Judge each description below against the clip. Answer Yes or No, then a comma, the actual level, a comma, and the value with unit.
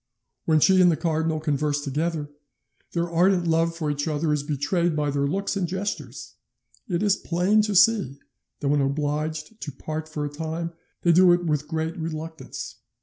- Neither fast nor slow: Yes, average, 180 wpm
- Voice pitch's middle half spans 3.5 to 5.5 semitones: No, average, 2.8 semitones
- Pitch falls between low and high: Yes, medium, 160 Hz